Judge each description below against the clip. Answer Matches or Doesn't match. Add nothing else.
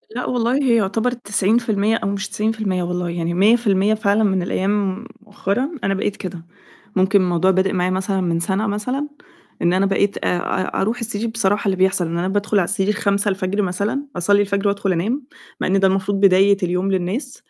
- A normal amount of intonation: Doesn't match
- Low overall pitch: Doesn't match